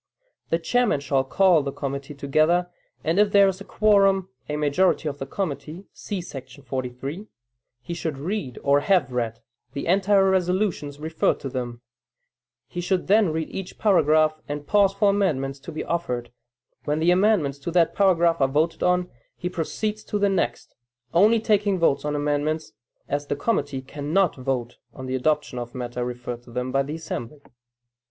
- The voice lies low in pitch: No, medium, 155 Hz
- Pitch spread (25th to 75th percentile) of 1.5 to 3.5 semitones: No, wide, 5.6 semitones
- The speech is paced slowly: No, average, 175 wpm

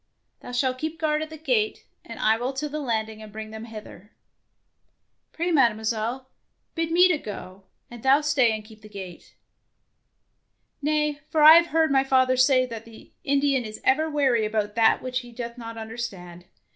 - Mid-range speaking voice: No, very high, 250 Hz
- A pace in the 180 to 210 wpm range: Yes, average, 185 wpm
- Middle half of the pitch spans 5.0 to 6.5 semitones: Yes, wide, 5.4 semitones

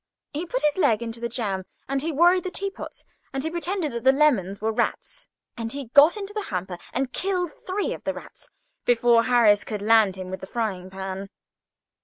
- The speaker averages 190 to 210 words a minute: Yes, average, 195 wpm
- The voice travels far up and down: Yes, wide, 7.7 semitones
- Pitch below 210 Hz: No, high, 240 Hz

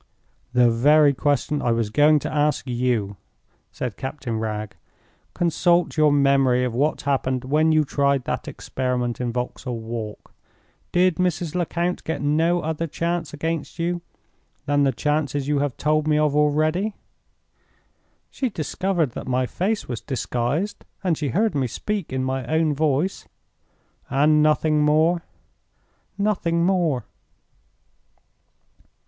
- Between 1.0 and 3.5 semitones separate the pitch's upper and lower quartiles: No, average, 4.3 semitones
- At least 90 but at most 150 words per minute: Yes, slow, 135 wpm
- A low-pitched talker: No, medium, 150 Hz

